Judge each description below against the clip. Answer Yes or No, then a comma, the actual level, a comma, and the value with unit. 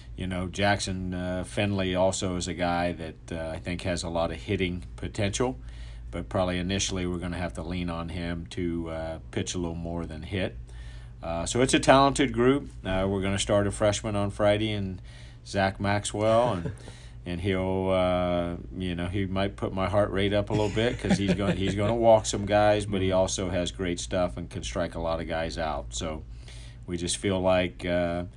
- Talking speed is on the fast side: Yes, fast, 215 wpm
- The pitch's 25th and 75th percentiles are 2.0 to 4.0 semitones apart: Yes, average, 2.8 semitones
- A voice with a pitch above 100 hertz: No, very low, 95 Hz